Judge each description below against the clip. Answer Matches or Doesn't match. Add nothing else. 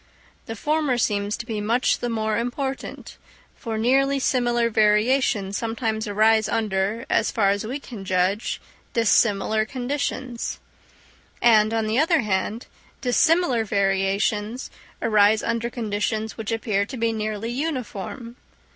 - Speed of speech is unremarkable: Doesn't match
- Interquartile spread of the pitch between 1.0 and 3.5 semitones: Matches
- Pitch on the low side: Doesn't match